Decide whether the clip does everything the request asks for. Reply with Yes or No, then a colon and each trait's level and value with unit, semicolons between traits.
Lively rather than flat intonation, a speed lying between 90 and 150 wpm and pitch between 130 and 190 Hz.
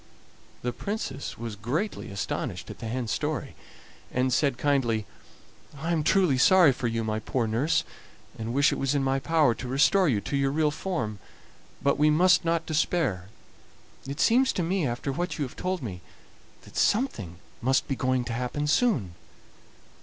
No: wide, 5.7 semitones; average, 175 wpm; low, 135 Hz